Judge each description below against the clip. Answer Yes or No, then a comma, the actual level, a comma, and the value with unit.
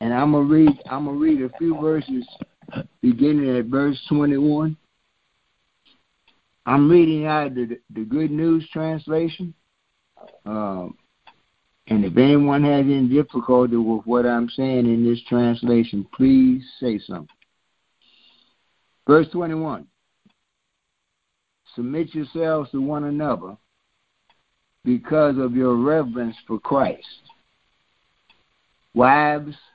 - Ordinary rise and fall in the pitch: Yes, average, 4.1 semitones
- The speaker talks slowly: Yes, slow, 110 wpm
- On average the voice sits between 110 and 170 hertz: Yes, medium, 140 Hz